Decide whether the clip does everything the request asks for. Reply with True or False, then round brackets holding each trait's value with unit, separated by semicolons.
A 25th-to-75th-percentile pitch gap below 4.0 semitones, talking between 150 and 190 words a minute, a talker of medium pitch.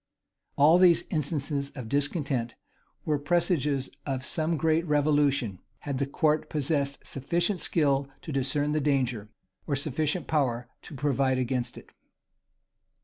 False (2.4 semitones; 135 wpm; 145 Hz)